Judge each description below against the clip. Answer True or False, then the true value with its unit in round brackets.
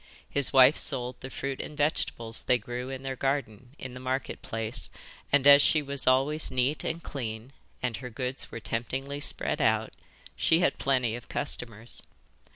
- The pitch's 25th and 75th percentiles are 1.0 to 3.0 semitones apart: True (2.4 semitones)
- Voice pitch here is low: True (130 Hz)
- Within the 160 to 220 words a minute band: True (170 wpm)